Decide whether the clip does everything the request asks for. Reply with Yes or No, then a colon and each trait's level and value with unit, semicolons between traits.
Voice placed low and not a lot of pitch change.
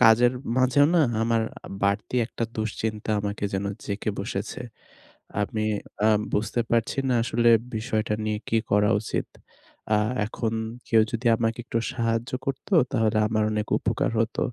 Yes: low, 110 Hz; narrow, 1.6 semitones